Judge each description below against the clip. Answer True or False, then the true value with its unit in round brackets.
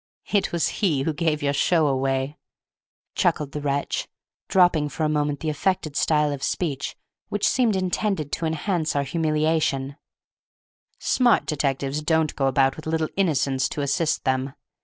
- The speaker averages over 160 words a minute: False (155 wpm)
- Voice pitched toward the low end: False (150 Hz)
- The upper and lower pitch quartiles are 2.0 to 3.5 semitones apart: True (2.7 semitones)